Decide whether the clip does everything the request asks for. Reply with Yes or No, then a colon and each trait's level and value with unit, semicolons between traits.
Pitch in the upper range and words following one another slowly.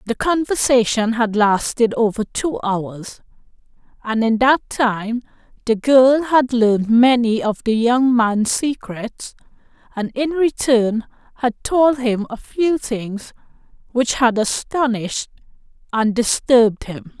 Yes: high, 235 Hz; slow, 125 wpm